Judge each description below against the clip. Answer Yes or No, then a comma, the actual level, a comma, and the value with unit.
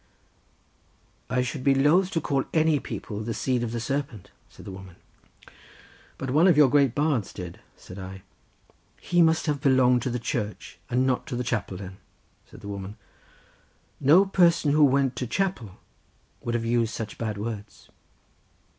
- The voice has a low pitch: Yes, low, 125 Hz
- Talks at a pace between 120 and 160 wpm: No, average, 170 wpm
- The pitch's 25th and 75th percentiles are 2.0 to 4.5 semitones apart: No, average, 5.0 semitones